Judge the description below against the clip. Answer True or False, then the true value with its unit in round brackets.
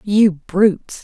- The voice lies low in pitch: False (195 Hz)